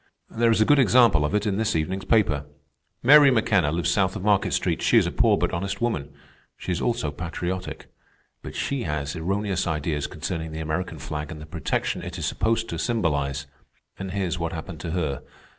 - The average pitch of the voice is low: Yes, very low, 90 Hz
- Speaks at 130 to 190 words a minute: No, average, 200 wpm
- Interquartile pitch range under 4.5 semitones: No, wide, 5.4 semitones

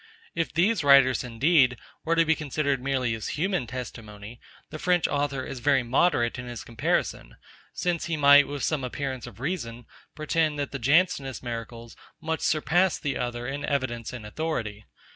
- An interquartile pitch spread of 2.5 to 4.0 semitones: No, average, 4.5 semitones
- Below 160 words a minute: No, average, 165 wpm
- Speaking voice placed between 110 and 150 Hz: Yes, low, 135 Hz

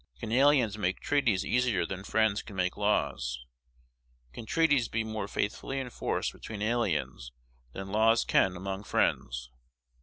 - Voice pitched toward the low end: Yes, low, 105 Hz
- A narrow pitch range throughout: No, average, 3.7 semitones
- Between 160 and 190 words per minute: No, average, 140 wpm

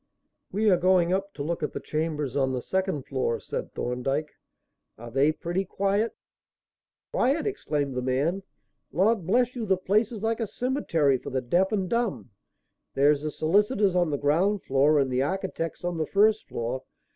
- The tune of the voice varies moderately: No, wide, 6.1 semitones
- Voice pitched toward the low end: No, medium, 170 Hz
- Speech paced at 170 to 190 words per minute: Yes, average, 180 wpm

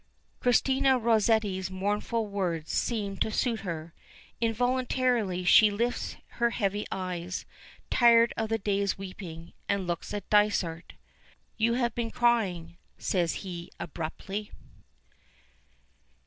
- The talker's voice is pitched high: Yes, high, 205 Hz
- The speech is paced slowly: Yes, slow, 110 wpm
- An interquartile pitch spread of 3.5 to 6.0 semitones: Yes, average, 4.2 semitones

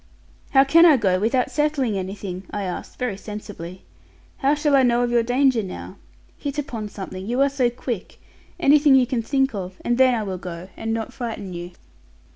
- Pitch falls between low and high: No, high, 235 Hz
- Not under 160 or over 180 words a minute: No, average, 195 wpm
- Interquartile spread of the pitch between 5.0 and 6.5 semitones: Yes, wide, 5.5 semitones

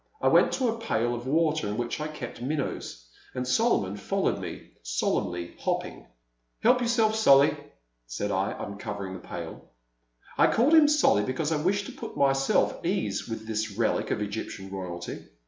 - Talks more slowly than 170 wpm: No, average, 175 wpm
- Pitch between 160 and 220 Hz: No, low, 125 Hz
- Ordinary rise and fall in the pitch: No, wide, 8.5 semitones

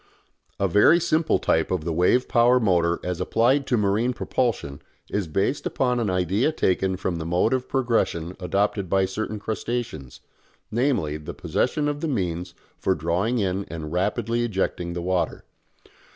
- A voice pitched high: No, low, 100 Hz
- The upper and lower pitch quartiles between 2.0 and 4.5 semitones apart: No, wide, 5.5 semitones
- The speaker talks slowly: No, average, 160 wpm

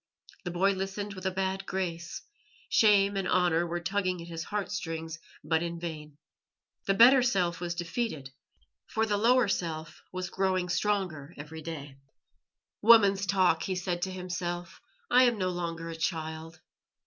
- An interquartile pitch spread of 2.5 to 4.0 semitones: Yes, average, 2.9 semitones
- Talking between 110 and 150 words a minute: No, average, 160 wpm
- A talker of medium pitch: Yes, medium, 180 Hz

